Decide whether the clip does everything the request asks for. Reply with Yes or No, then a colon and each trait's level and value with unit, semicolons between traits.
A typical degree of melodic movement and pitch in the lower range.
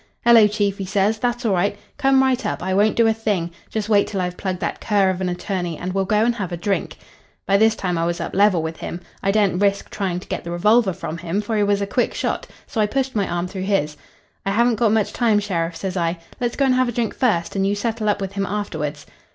No: average, 3.3 semitones; high, 200 Hz